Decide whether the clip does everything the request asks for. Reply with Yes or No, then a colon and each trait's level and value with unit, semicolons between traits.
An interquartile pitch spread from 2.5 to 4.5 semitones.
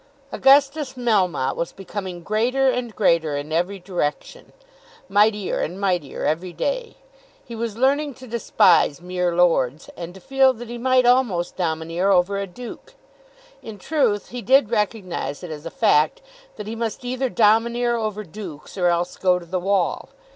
No: wide, 5.5 semitones